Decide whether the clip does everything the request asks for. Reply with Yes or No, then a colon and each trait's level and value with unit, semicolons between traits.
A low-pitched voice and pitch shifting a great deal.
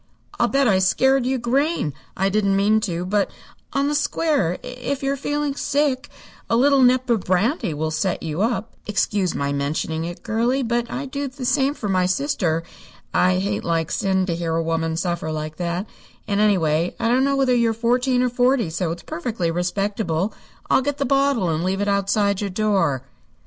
No: high, 205 Hz; wide, 6.6 semitones